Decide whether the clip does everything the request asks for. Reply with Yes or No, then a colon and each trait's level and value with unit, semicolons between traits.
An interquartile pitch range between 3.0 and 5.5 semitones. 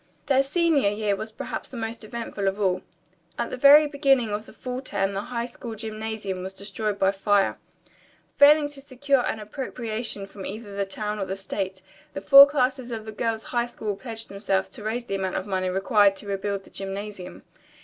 Yes: average, 3.8 semitones